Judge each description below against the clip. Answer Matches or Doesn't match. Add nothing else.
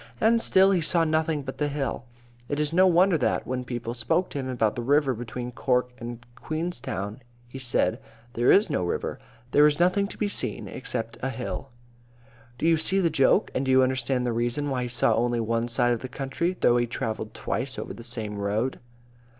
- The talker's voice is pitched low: Matches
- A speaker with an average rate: Doesn't match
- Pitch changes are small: Doesn't match